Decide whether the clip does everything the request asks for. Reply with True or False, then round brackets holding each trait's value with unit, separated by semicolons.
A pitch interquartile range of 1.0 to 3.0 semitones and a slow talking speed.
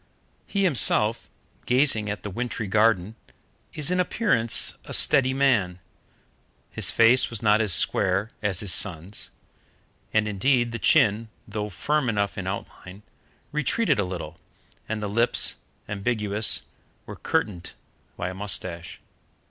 False (3.6 semitones; 130 wpm)